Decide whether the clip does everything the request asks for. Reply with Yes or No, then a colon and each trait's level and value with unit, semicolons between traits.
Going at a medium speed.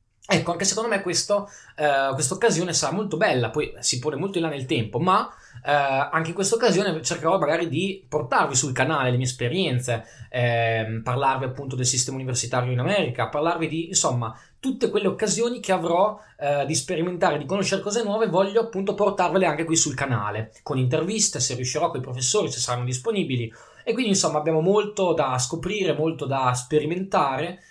No: fast, 180 wpm